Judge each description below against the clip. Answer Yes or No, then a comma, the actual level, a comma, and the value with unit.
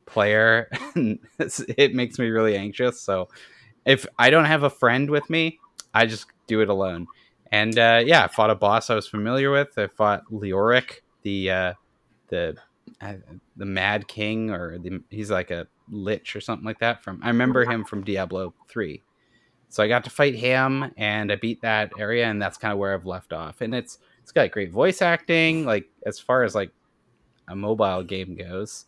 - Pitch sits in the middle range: No, low, 110 Hz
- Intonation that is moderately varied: Yes, average, 3.7 semitones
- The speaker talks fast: No, average, 195 wpm